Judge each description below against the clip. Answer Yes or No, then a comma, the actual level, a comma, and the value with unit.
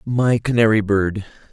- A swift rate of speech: No, slow, 120 wpm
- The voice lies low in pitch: Yes, low, 110 Hz